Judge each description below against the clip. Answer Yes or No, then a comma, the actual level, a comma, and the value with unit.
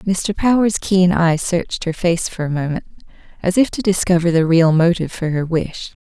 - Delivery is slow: No, average, 200 wpm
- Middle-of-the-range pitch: Yes, medium, 175 Hz